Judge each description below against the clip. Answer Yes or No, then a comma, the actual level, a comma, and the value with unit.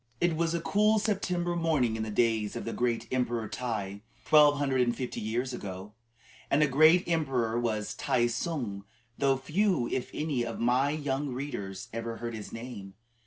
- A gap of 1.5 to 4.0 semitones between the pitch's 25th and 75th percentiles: No, average, 5.0 semitones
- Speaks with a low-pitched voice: Yes, low, 125 Hz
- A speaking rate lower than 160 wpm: No, average, 175 wpm